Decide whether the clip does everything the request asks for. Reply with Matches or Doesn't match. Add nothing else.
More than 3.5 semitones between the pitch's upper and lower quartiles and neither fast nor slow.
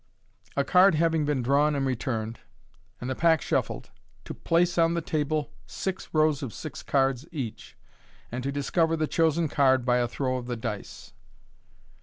Matches